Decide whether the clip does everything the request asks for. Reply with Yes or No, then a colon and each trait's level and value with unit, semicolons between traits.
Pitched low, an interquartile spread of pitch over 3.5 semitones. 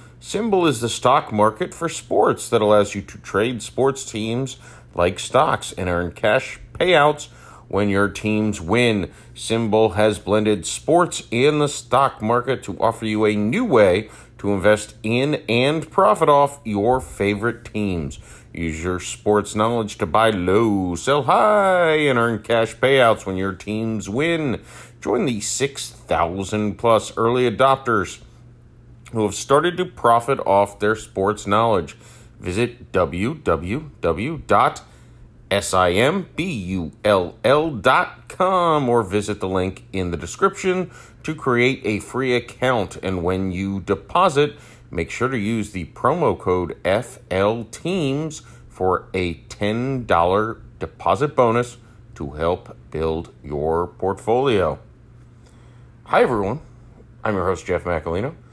Yes: low, 115 Hz; average, 4.0 semitones